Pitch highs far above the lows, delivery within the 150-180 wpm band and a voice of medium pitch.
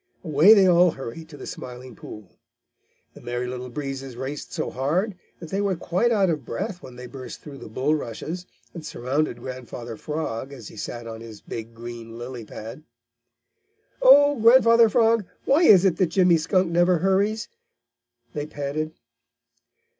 Yes: wide, 7.0 semitones; average, 160 wpm; medium, 150 Hz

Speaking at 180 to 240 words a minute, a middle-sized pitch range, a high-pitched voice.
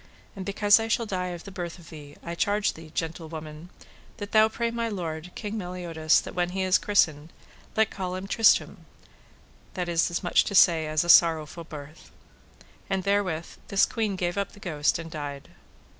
No: average, 190 wpm; average, 3.8 semitones; medium, 180 Hz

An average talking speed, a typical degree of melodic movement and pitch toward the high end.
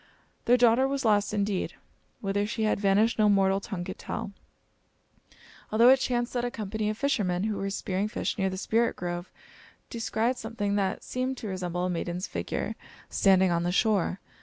Yes: average, 180 wpm; average, 3.3 semitones; high, 205 Hz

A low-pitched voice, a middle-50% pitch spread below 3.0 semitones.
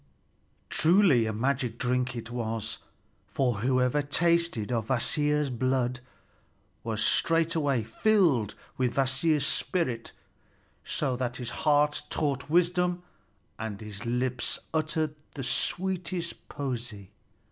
No: low, 130 Hz; average, 4.8 semitones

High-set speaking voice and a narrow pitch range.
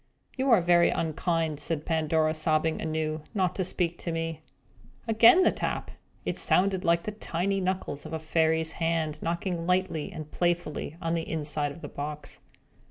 No: medium, 165 Hz; narrow, 2.3 semitones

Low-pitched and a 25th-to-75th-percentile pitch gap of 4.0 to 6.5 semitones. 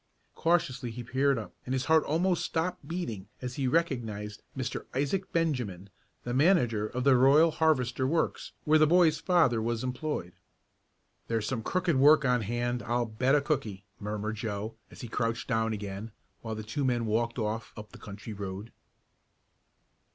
Yes: low, 125 Hz; average, 5.3 semitones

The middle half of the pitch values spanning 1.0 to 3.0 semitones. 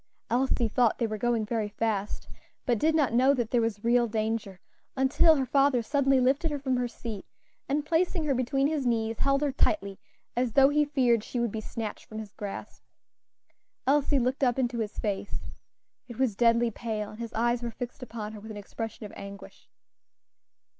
No: average, 3.5 semitones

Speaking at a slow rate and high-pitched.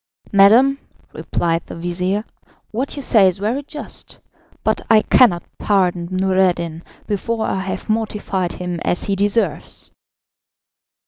Yes: slow, 125 wpm; high, 195 Hz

